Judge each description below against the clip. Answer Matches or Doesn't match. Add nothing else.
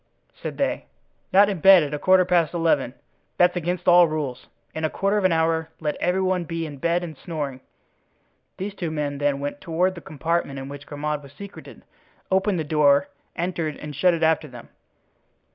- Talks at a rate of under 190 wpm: Doesn't match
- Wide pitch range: Doesn't match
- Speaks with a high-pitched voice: Doesn't match